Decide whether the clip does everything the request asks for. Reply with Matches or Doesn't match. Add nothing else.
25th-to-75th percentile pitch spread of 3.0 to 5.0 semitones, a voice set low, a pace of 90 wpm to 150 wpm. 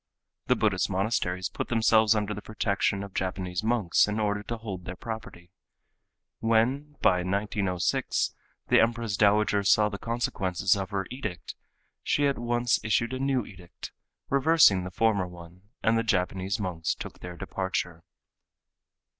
Matches